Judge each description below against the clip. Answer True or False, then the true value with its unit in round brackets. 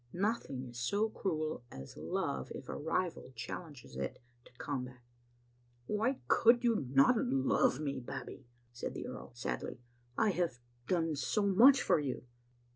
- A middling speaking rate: True (150 wpm)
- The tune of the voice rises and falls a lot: True (8.3 semitones)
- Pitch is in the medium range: True (145 Hz)